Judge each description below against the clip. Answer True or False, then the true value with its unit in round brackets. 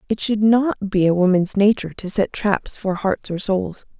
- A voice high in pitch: True (200 Hz)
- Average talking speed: False (210 wpm)